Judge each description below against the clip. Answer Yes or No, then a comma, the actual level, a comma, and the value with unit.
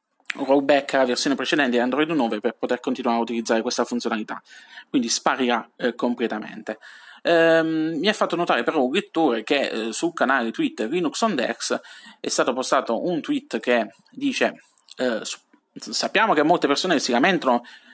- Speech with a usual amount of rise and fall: No, wide, 7.5 semitones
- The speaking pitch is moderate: Yes, medium, 145 Hz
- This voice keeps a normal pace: Yes, average, 155 wpm